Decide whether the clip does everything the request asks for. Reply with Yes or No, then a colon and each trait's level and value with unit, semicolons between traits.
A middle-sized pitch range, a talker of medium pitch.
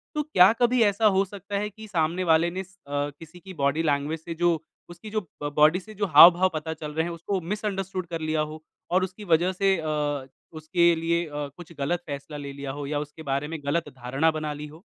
Yes: average, 3.6 semitones; medium, 165 Hz